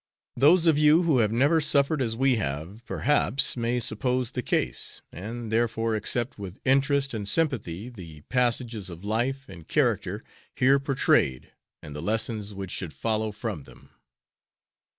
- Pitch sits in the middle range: No, low, 115 Hz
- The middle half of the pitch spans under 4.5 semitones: No, average, 4.8 semitones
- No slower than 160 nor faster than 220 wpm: No, average, 150 wpm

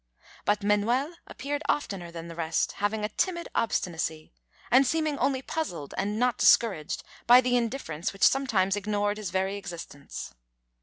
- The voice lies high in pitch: Yes, high, 210 Hz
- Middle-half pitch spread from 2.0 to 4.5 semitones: No, average, 5.3 semitones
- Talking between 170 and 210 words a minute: No, average, 150 wpm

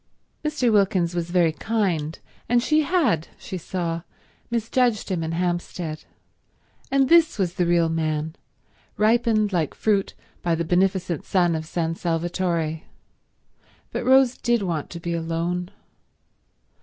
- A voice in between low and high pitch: Yes, medium, 175 Hz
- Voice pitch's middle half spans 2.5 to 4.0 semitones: No, average, 4.6 semitones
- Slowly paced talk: Yes, slow, 130 wpm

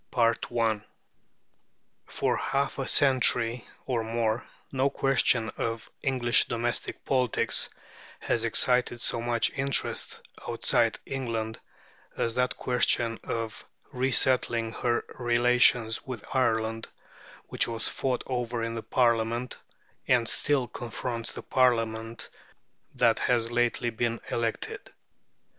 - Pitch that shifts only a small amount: Yes, narrow, 1.7 semitones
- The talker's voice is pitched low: Yes, low, 120 Hz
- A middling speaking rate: No, slow, 110 wpm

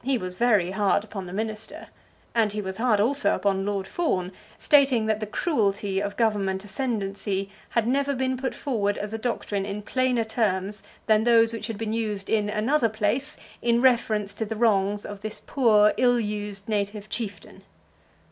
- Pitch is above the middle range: Yes, high, 215 Hz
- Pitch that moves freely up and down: No, average, 2.7 semitones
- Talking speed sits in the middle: Yes, average, 175 wpm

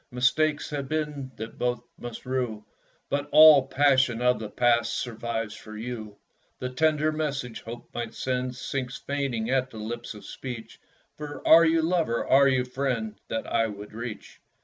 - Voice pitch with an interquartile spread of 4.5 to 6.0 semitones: No, average, 3.6 semitones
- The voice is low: Yes, low, 125 Hz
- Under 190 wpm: Yes, average, 170 wpm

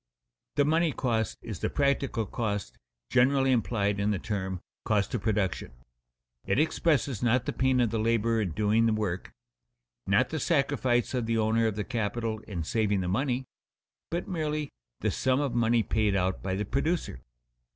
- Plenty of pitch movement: No, average, 4.2 semitones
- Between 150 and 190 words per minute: Yes, average, 170 wpm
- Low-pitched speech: Yes, low, 115 Hz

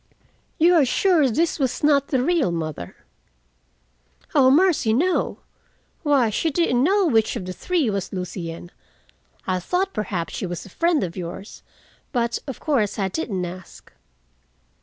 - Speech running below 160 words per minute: Yes, average, 150 wpm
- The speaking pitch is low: No, high, 245 Hz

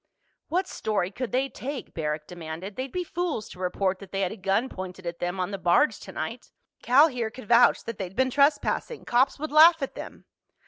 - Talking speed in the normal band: No, fast, 210 wpm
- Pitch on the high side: Yes, high, 220 Hz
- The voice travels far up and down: Yes, wide, 6.7 semitones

